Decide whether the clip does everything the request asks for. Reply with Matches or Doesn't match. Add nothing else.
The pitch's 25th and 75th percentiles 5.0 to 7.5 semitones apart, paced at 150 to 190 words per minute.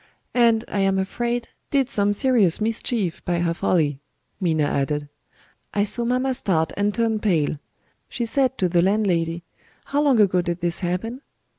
Matches